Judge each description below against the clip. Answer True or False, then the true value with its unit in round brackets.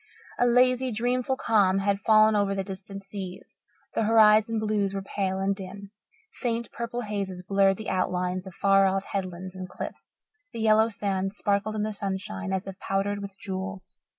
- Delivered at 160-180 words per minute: True (175 wpm)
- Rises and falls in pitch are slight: True (2.2 semitones)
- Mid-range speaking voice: False (200 Hz)